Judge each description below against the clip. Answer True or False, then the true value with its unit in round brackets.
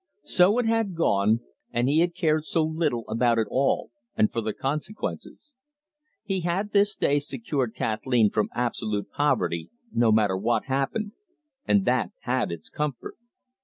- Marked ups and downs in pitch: True (7.2 semitones)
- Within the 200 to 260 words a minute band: False (155 wpm)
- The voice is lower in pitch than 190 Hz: True (135 Hz)